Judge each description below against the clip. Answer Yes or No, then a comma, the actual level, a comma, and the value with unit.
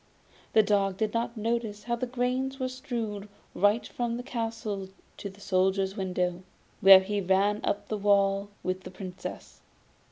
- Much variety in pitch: No, average, 3.2 semitones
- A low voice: No, high, 205 Hz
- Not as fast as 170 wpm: Yes, average, 160 wpm